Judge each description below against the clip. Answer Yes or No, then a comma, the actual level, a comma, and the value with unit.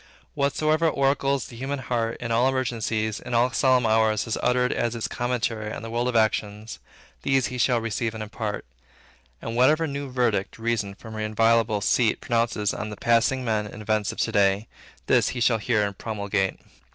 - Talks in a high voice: No, low, 115 Hz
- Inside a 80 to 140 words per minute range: No, average, 190 wpm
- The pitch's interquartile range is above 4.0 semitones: No, narrow, 2.6 semitones